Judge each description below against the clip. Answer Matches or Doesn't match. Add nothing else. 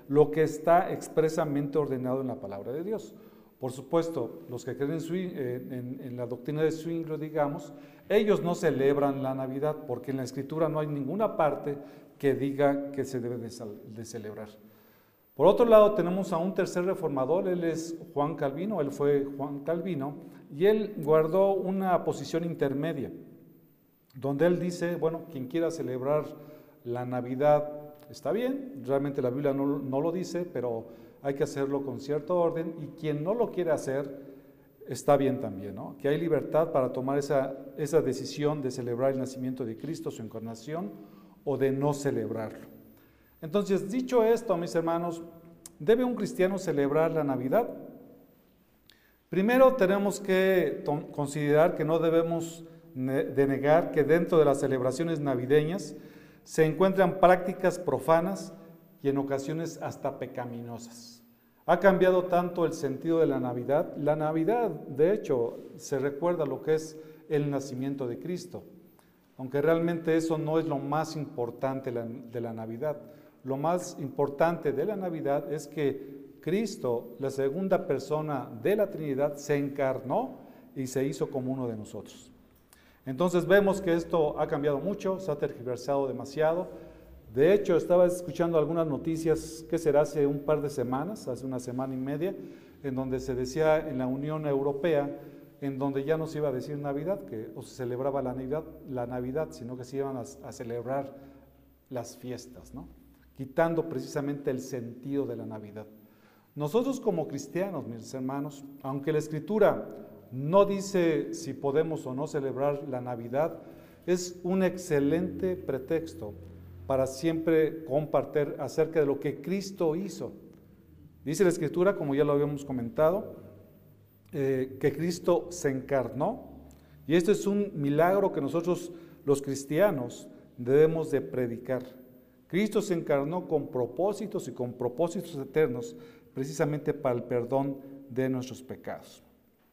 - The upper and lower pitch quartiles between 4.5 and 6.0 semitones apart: Doesn't match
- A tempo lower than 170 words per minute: Matches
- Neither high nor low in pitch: Matches